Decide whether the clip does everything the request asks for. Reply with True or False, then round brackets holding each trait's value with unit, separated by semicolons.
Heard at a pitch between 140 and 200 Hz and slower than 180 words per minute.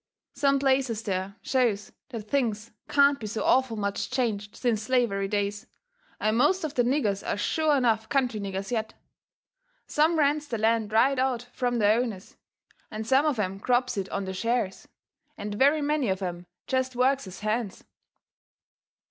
False (230 Hz; 165 wpm)